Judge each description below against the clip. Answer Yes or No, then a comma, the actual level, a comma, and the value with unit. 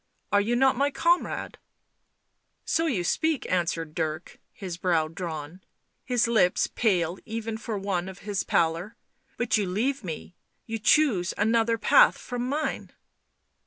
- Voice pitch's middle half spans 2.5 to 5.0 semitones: No, wide, 5.5 semitones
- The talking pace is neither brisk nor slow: Yes, average, 155 wpm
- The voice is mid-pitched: No, high, 205 Hz